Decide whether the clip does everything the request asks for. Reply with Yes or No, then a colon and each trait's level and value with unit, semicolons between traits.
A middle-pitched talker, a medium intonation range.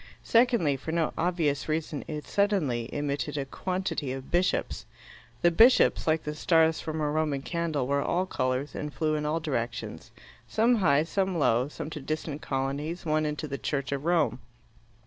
Yes: medium, 155 Hz; average, 3.1 semitones